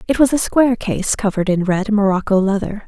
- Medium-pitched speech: No, high, 210 Hz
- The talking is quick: Yes, fast, 210 wpm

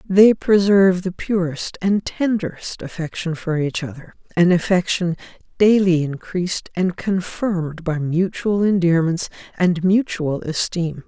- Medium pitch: Yes, medium, 180 Hz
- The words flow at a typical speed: No, slow, 120 wpm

